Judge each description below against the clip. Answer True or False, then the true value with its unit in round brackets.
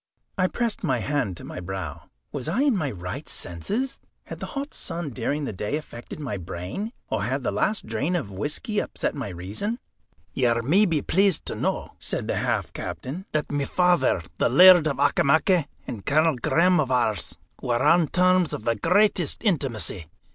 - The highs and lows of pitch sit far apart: True (8.2 semitones)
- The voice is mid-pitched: True (145 Hz)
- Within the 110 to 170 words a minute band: False (185 wpm)